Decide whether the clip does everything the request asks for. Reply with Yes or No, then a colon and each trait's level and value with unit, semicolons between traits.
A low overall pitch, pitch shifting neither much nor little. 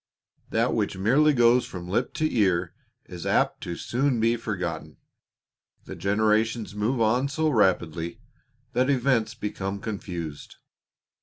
Yes: low, 110 Hz; average, 4.7 semitones